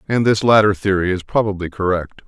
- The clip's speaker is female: No, male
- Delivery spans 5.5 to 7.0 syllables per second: Yes, 5.8 syllables/s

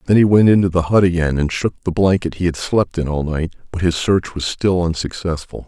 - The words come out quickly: Yes, fast, 245 wpm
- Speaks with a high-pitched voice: No, very low, 85 Hz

